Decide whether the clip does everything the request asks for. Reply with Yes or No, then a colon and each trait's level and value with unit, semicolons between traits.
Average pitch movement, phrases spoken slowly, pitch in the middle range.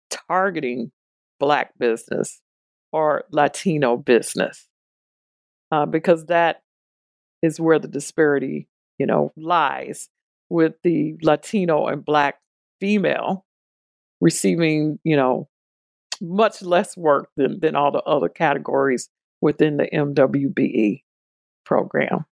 Yes: average, 3.5 semitones; slow, 100 wpm; medium, 150 Hz